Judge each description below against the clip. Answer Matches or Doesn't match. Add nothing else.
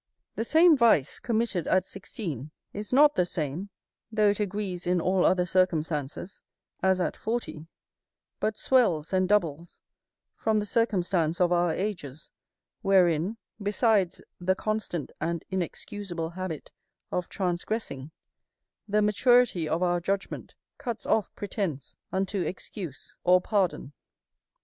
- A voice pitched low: Doesn't match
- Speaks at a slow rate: Matches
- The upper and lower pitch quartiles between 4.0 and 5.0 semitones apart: Doesn't match